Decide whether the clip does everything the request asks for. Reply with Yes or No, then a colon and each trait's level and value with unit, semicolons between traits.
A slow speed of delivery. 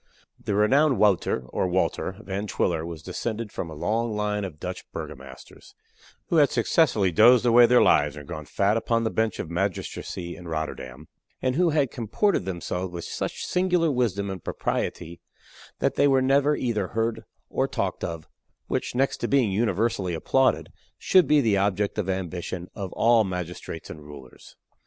No: average, 170 wpm